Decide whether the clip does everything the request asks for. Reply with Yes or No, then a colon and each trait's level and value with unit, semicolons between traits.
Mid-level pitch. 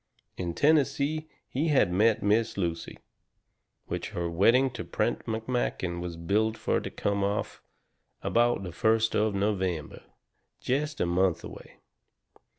No: low, 105 Hz